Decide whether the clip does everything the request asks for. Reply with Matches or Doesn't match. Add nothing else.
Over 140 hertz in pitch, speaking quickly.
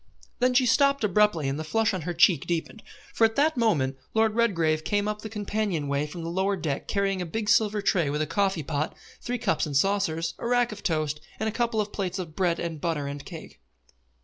Matches